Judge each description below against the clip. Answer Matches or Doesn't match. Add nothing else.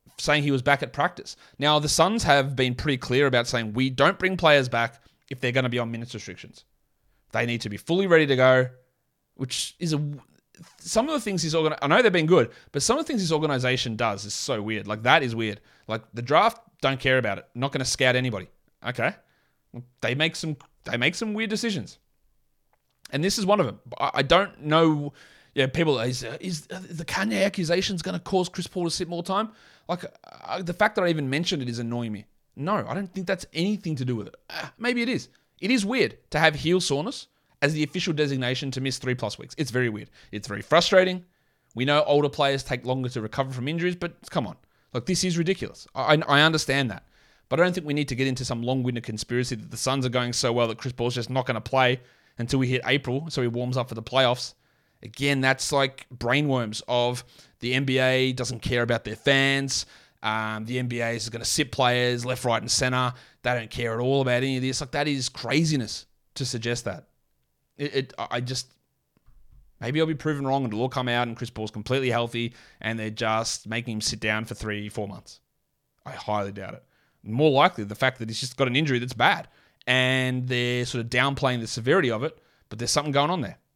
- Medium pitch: Doesn't match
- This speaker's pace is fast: Matches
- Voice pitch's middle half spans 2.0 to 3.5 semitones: Doesn't match